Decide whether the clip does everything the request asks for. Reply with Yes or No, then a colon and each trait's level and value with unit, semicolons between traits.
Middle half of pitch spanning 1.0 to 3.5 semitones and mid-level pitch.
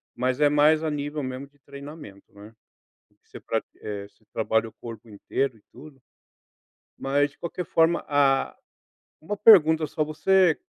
No: average, 4.0 semitones; medium, 145 Hz